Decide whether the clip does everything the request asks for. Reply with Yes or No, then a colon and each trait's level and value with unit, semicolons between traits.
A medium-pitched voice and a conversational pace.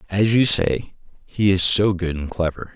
No: very low, 95 Hz; average, 195 wpm